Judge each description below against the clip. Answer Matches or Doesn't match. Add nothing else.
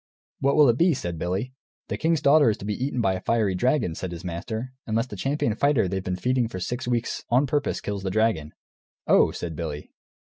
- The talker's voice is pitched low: Matches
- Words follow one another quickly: Matches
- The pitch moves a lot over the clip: Matches